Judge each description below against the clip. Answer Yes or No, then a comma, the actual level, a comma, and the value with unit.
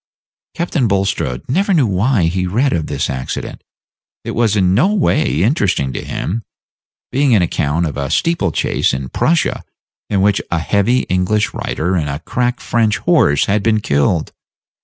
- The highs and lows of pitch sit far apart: Yes, wide, 6.8 semitones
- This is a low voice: Yes, low, 100 Hz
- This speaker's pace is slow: No, average, 165 wpm